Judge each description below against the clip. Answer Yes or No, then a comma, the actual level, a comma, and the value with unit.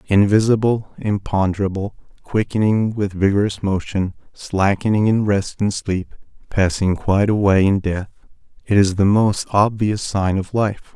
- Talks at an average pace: No, slow, 130 wpm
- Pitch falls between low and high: No, low, 100 Hz